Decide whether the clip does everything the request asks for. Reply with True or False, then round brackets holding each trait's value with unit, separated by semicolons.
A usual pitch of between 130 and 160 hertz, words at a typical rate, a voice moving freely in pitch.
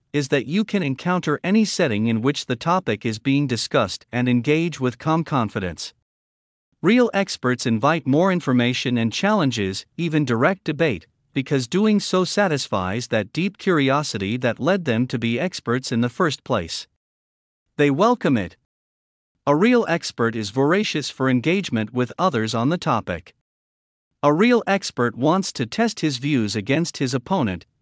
True (135 Hz; 155 wpm; 6.7 semitones)